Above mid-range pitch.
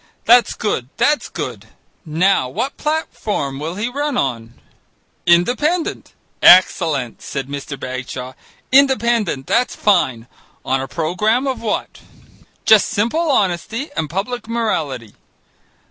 Yes: high, 195 Hz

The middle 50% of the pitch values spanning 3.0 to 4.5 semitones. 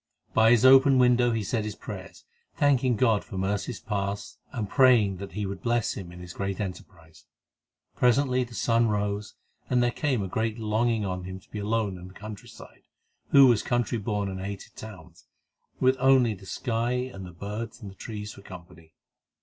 Yes: average, 3.8 semitones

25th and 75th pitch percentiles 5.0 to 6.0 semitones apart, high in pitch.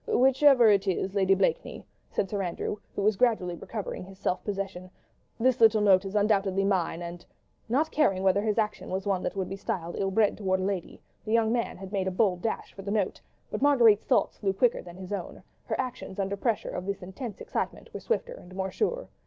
No: average, 3.0 semitones; high, 200 Hz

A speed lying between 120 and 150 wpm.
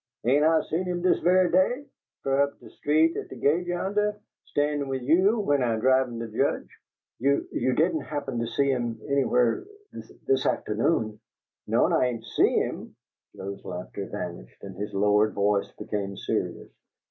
No: average, 170 wpm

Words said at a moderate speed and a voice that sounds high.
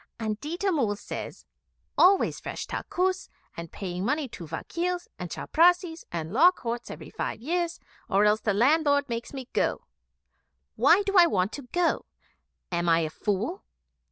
Yes: average, 155 wpm; very high, 265 Hz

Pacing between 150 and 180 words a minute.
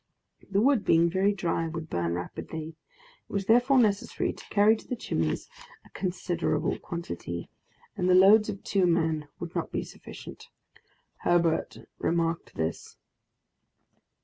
No: average, 140 wpm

